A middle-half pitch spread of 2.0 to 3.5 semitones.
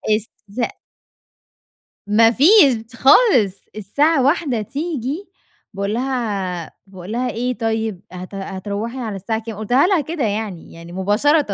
No: average, 4.9 semitones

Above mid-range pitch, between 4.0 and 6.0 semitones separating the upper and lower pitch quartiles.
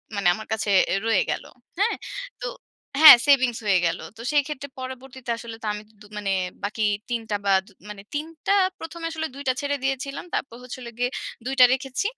Yes: very high, 255 Hz; average, 4.6 semitones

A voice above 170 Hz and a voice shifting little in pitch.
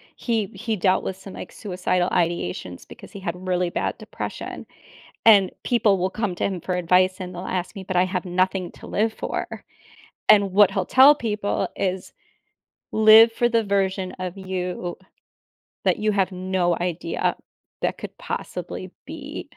Yes: high, 190 Hz; narrow, 2.3 semitones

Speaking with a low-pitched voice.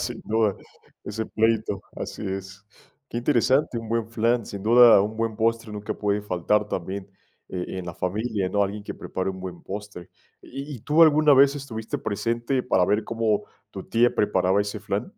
Yes: low, 110 Hz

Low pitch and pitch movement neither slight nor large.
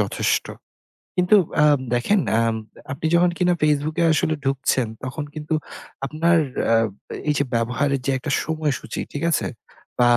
No: medium, 150 Hz; average, 3.0 semitones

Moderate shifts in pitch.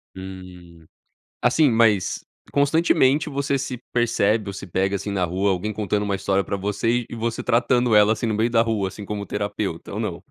Yes: average, 3.4 semitones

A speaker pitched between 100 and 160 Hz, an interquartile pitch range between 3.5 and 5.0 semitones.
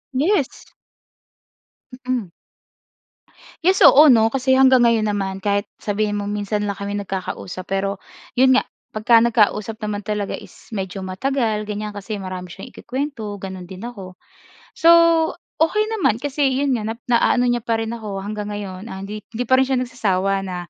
No: high, 215 Hz; average, 4.0 semitones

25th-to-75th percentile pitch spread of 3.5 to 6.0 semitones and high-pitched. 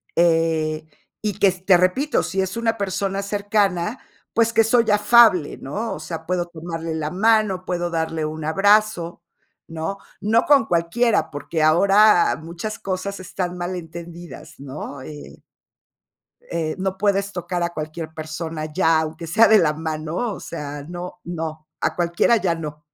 No: average, 3.8 semitones; medium, 175 Hz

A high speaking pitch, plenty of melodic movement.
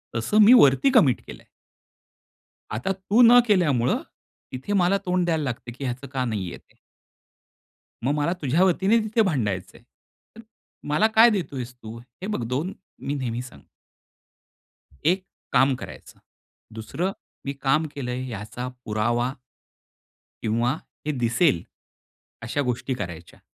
No: low, 135 Hz; wide, 7.4 semitones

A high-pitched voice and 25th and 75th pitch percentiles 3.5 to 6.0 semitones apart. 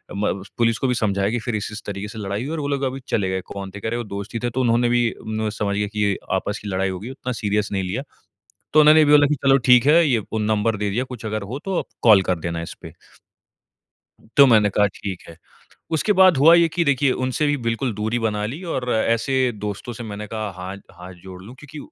No: low, 110 Hz; average, 4.2 semitones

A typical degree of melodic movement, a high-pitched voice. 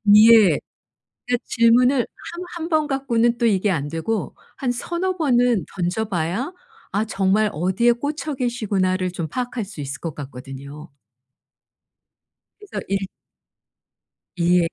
No: wide, 5.8 semitones; high, 220 Hz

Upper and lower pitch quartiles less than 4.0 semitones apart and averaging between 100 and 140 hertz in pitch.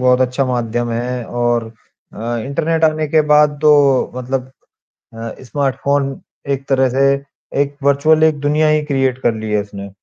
Yes: average, 3.2 semitones; low, 135 Hz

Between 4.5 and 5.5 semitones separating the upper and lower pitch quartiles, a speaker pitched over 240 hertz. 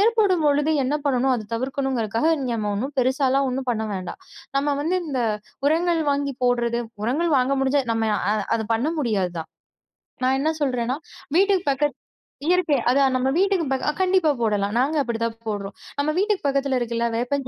No: average, 4.0 semitones; very high, 270 Hz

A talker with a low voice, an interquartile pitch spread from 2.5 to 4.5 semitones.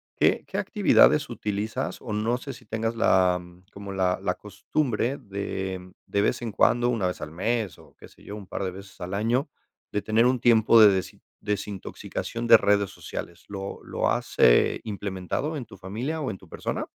Yes: low, 105 Hz; average, 3.4 semitones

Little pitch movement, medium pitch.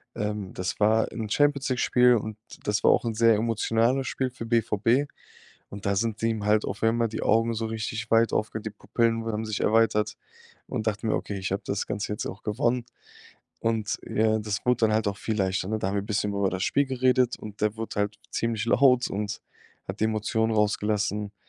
No: narrow, 1.7 semitones; low, 110 Hz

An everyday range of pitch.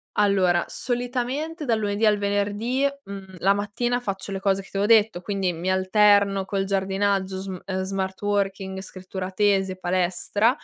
No: narrow, 1.6 semitones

